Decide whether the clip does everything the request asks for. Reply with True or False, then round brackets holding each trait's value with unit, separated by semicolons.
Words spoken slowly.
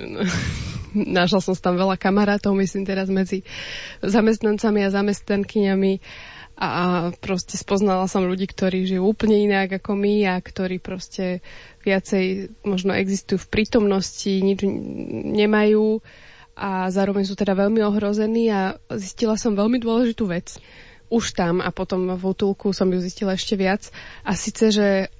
False (140 wpm)